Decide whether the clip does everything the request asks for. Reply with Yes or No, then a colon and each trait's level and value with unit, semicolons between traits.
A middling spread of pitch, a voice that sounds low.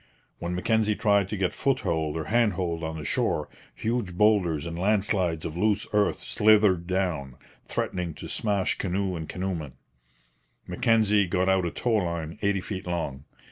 Yes: average, 3.7 semitones; very low, 95 Hz